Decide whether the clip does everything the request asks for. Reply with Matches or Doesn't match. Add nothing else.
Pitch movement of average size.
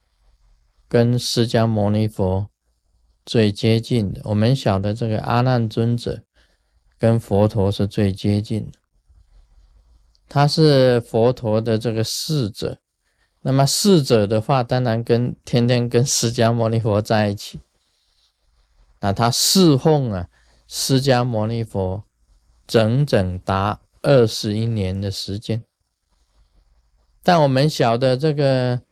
Matches